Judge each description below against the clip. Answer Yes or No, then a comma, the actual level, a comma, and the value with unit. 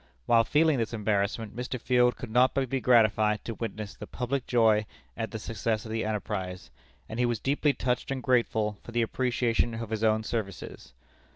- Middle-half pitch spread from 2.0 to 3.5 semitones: Yes, narrow, 2.4 semitones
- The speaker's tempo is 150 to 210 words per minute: Yes, average, 190 wpm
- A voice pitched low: Yes, low, 115 Hz